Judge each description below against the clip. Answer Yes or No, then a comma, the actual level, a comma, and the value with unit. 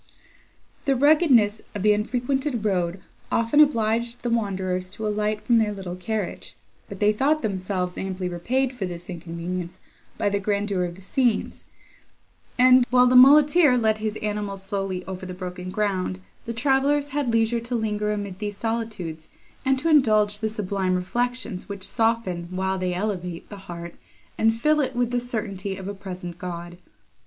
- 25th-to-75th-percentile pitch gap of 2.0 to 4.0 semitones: No, average, 4.5 semitones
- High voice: Yes, high, 210 Hz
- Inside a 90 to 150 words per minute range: No, average, 165 wpm